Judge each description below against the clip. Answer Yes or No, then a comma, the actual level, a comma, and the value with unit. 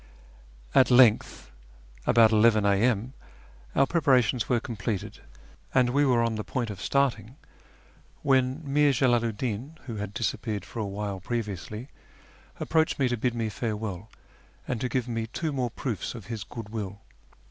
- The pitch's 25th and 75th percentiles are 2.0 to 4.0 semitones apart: Yes, average, 3.3 semitones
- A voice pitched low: Yes, low, 115 Hz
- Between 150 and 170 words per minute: Yes, average, 160 wpm